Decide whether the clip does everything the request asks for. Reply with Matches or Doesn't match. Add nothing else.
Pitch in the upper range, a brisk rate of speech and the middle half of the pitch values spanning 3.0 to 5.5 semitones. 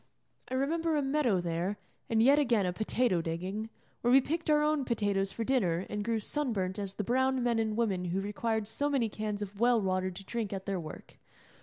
Matches